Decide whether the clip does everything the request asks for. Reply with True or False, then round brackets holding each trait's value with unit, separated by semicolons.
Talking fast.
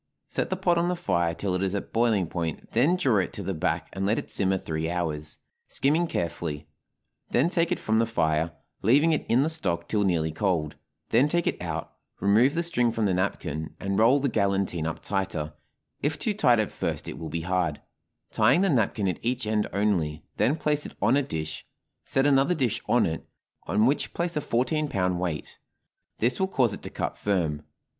True (210 wpm)